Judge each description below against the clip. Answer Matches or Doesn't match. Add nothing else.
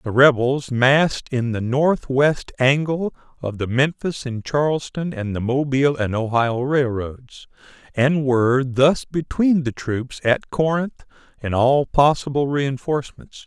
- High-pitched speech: Doesn't match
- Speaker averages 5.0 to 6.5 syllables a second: Doesn't match